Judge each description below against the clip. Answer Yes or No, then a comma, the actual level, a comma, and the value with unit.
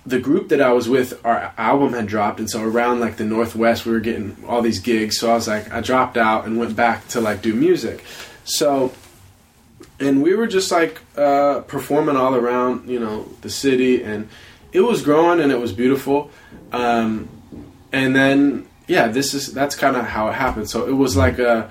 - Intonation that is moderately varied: Yes, average, 3.5 semitones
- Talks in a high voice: No, low, 120 Hz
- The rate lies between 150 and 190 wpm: No, fast, 205 wpm